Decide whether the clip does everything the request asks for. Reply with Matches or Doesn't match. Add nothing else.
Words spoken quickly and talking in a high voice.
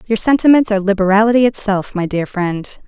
Doesn't match